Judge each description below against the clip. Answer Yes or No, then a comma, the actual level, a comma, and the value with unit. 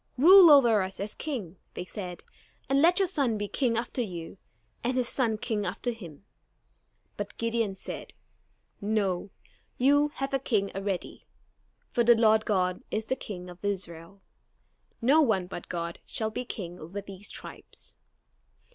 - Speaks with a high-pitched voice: Yes, high, 215 Hz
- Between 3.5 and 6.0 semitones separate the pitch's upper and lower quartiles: Yes, average, 4.8 semitones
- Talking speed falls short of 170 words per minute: Yes, average, 155 wpm